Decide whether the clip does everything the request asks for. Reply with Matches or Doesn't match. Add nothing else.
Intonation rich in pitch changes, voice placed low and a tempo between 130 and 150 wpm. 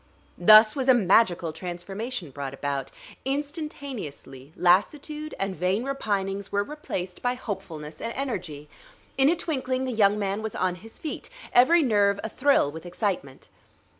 Doesn't match